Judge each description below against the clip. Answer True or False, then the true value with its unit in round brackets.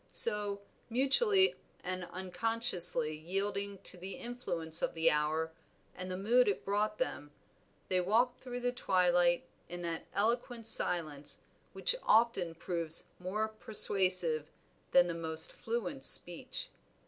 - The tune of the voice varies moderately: True (5.0 semitones)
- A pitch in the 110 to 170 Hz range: False (190 Hz)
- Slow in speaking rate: True (125 wpm)